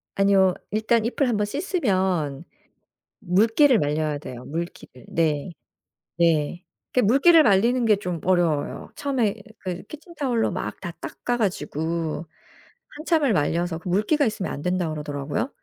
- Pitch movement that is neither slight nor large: No, wide, 6.5 semitones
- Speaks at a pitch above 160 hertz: Yes, high, 190 Hz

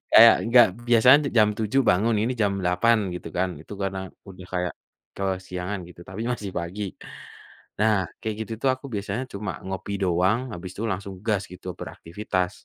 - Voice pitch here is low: Yes, low, 100 Hz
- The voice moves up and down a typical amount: Yes, average, 3.3 semitones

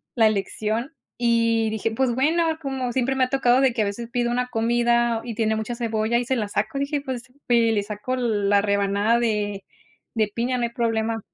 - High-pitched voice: Yes, high, 235 Hz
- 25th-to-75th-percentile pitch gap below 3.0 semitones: Yes, narrow, 2.4 semitones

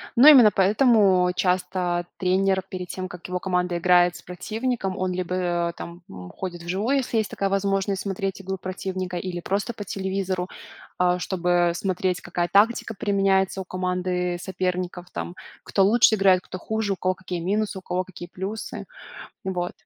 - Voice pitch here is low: No, medium, 185 Hz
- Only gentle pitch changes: Yes, narrow, 1.6 semitones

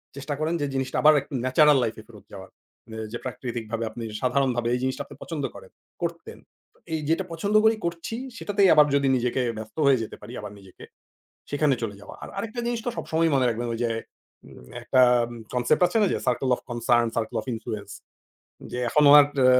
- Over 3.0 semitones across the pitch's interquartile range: Yes, average, 4.7 semitones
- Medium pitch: No, low, 130 Hz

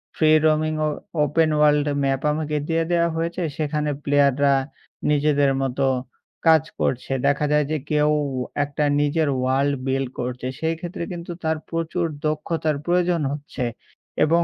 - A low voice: No, medium, 150 Hz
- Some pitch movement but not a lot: No, narrow, 2.3 semitones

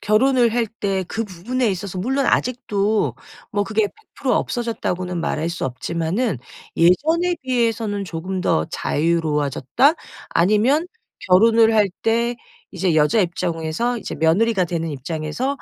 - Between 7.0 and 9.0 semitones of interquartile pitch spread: No, wide, 5.6 semitones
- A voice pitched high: Yes, high, 200 Hz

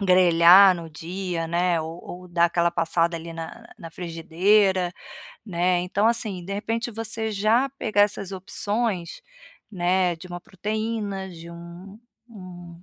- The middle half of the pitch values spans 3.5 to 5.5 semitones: No, average, 3.0 semitones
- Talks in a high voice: No, medium, 180 Hz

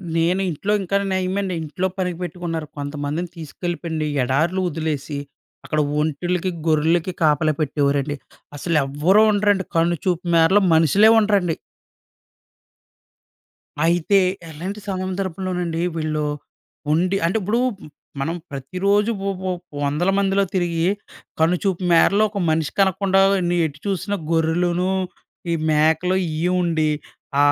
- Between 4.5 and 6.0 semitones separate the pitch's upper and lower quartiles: No, average, 3.2 semitones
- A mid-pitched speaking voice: Yes, medium, 175 Hz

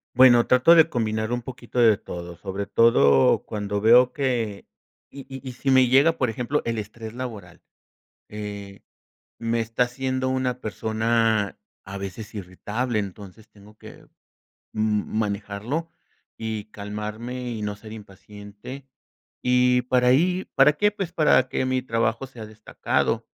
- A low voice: Yes, low, 115 Hz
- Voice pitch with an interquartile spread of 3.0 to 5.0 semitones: Yes, average, 3.5 semitones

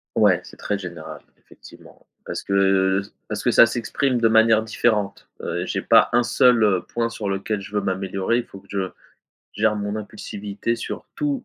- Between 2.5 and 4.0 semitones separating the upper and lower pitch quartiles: Yes, average, 2.9 semitones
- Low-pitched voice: Yes, low, 105 Hz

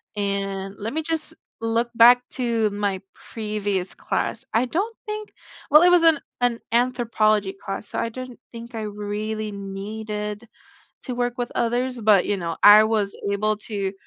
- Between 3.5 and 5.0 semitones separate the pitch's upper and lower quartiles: No, average, 3.1 semitones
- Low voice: No, high, 220 Hz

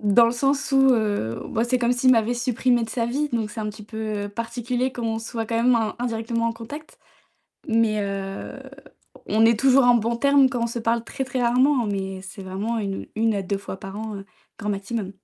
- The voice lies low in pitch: No, high, 230 Hz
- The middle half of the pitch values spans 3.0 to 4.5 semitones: No, narrow, 2.6 semitones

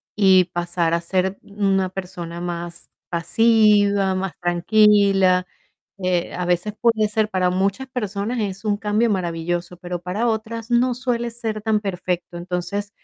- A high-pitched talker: Yes, high, 195 Hz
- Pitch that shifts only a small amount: No, average, 3.2 semitones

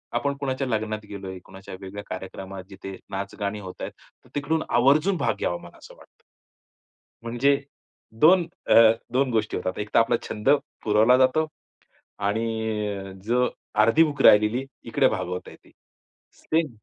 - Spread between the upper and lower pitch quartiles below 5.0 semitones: No, average, 5.3 semitones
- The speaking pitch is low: Yes, low, 110 Hz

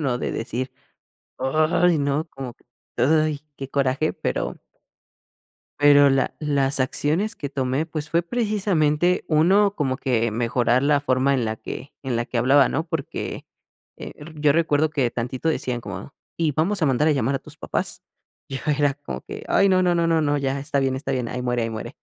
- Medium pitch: Yes, medium, 145 Hz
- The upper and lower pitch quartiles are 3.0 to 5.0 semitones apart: Yes, average, 3.4 semitones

